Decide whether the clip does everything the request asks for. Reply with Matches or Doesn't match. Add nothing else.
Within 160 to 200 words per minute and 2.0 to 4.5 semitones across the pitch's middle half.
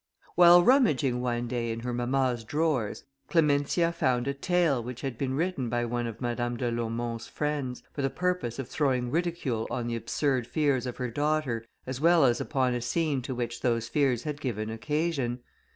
Matches